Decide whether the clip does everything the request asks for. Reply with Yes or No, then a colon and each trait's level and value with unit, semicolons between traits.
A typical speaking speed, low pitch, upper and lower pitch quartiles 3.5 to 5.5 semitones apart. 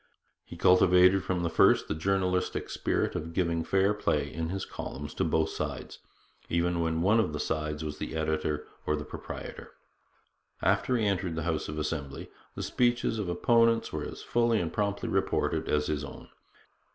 Yes: average, 175 wpm; very low, 85 Hz; average, 4.0 semitones